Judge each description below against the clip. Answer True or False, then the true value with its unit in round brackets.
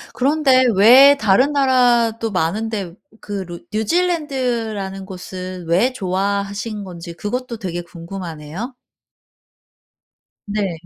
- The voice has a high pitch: True (205 Hz)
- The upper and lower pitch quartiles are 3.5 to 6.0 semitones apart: True (5.1 semitones)